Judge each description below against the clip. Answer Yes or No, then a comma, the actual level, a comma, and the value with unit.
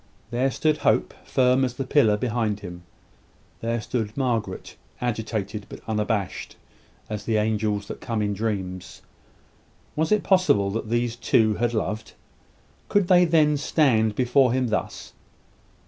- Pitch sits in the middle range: No, low, 115 Hz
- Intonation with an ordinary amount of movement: Yes, average, 3.6 semitones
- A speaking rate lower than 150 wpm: Yes, average, 140 wpm